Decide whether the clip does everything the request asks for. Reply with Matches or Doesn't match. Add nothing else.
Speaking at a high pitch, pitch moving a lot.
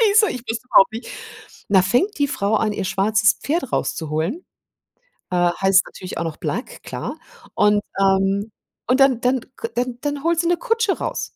Matches